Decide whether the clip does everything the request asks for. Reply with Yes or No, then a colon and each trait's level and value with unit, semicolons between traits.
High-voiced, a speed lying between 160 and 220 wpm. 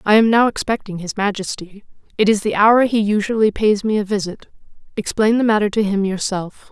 Yes: high, 210 Hz; average, 195 wpm